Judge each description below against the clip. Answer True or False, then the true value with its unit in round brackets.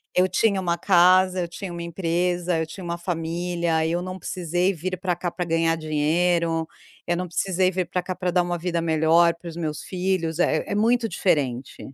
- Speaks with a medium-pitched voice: True (175 Hz)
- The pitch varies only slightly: True (1.8 semitones)